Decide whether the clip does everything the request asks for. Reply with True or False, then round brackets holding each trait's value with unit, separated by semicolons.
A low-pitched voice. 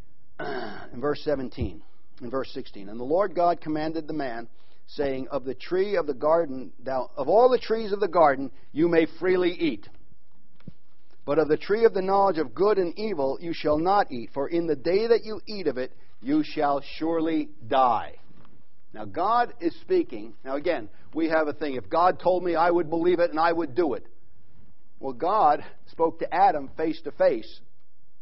False (165 Hz)